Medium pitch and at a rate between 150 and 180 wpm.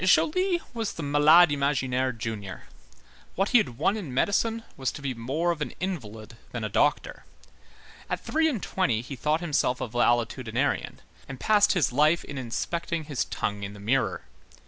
Yes: medium, 145 Hz; average, 170 wpm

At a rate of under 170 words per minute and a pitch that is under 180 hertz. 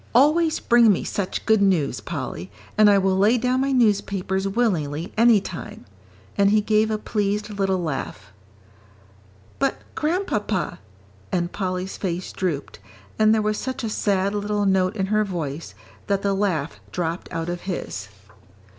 No: average, 155 wpm; high, 200 Hz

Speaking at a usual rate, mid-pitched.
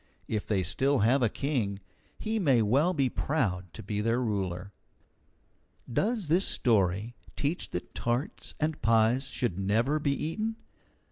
No: average, 145 wpm; low, 120 Hz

